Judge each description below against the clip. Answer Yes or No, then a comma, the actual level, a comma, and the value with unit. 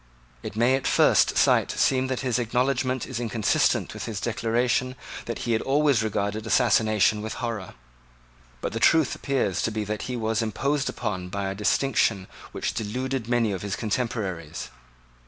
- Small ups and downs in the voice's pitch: No, average, 3.4 semitones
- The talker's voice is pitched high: No, low, 115 Hz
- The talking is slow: No, average, 165 wpm